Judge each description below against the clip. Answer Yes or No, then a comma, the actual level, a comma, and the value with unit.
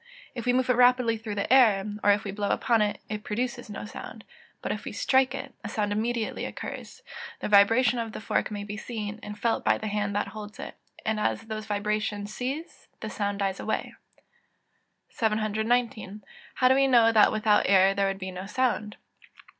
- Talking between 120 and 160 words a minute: No, average, 200 wpm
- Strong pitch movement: No, narrow, 2.6 semitones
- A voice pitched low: No, high, 215 Hz